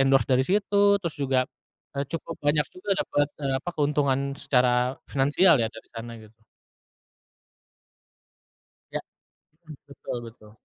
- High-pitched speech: No, medium, 140 Hz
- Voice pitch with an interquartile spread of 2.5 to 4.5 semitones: Yes, average, 3.6 semitones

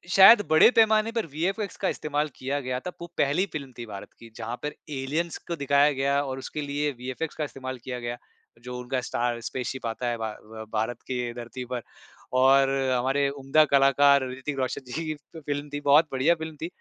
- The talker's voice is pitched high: No, low, 135 Hz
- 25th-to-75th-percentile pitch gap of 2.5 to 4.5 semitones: Yes, average, 3.3 semitones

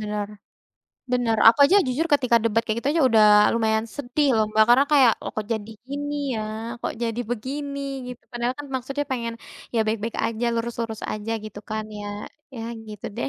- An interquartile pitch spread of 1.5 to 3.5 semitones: Yes, average, 3.0 semitones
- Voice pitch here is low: No, high, 230 Hz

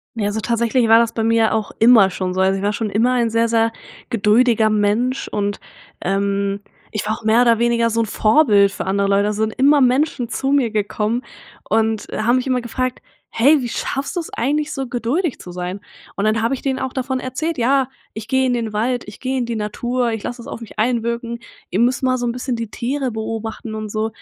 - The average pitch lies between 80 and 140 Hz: No, high, 230 Hz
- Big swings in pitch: No, average, 2.8 semitones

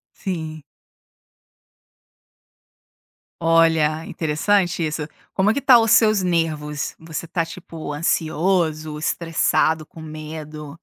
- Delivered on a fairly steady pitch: Yes, narrow, 2.0 semitones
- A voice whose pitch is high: No, medium, 160 Hz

